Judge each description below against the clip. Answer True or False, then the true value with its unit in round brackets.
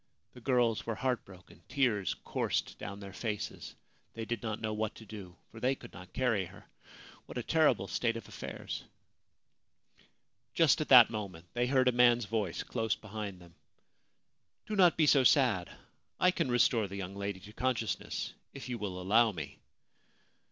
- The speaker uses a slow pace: False (175 wpm)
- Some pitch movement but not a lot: True (3.9 semitones)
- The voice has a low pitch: True (110 Hz)